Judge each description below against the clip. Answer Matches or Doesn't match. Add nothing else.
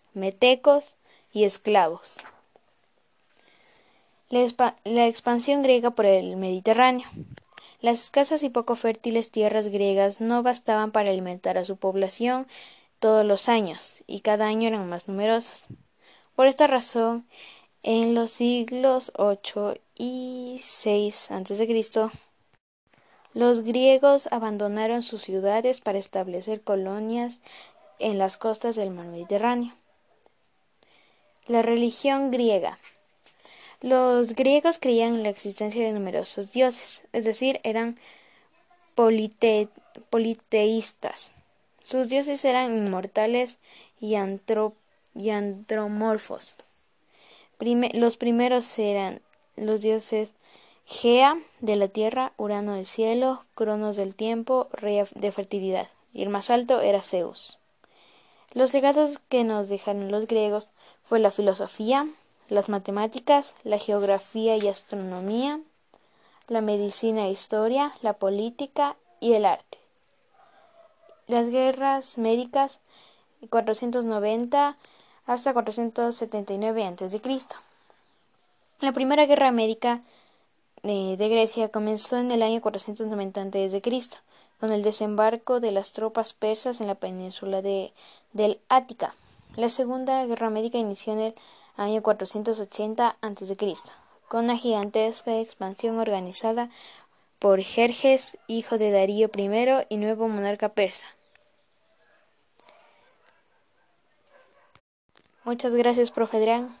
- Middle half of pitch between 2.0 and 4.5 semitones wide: Matches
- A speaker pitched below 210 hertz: Doesn't match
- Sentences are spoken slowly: Matches